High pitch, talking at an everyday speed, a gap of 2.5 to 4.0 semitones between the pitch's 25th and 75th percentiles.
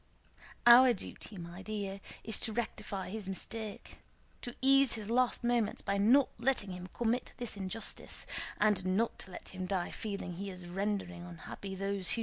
Yes: high, 200 Hz; average, 170 wpm; average, 3.6 semitones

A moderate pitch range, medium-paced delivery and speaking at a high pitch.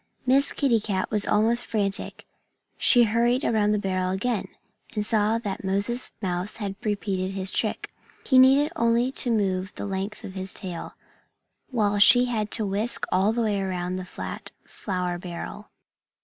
Yes: average, 3.5 semitones; average, 165 wpm; high, 205 Hz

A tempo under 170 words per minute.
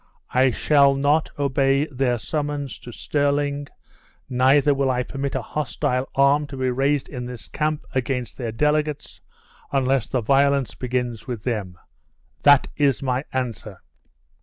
Yes: average, 140 wpm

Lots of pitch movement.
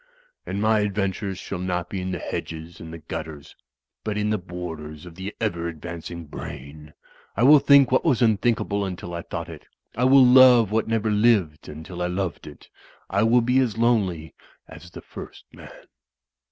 No: average, 5.0 semitones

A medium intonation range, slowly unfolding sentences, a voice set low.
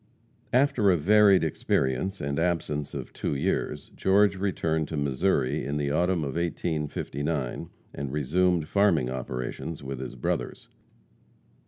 Yes: average, 4.8 semitones; slow, 130 wpm; very low, 80 Hz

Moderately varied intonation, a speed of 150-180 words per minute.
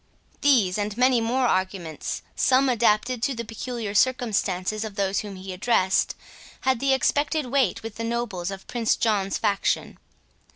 Yes: average, 4.2 semitones; average, 155 wpm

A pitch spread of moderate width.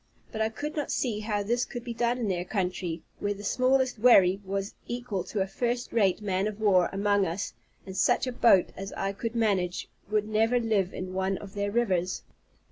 Yes: average, 3.5 semitones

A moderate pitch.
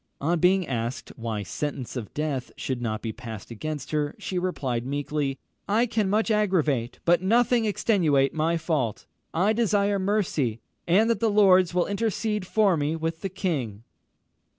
Yes: medium, 165 Hz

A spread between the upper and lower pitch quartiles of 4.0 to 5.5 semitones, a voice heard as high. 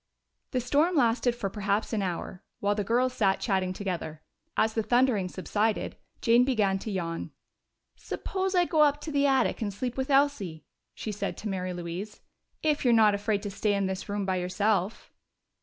Yes: average, 4.7 semitones; high, 210 Hz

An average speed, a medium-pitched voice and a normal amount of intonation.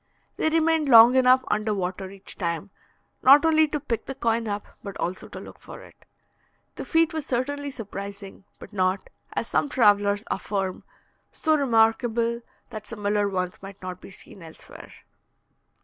No: average, 160 wpm; high, 220 Hz; average, 5.0 semitones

